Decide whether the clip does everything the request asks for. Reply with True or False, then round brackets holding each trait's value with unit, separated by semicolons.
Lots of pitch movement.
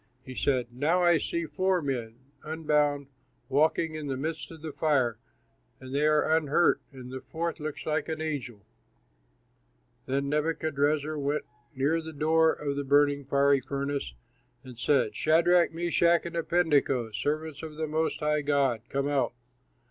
False (2.4 semitones)